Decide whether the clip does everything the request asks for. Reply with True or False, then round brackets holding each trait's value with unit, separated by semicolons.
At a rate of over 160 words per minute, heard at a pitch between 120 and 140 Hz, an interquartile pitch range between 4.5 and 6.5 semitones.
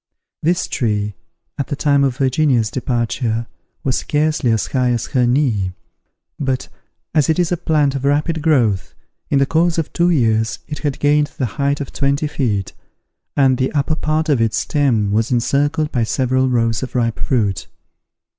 False (175 wpm; 135 Hz; 4.1 semitones)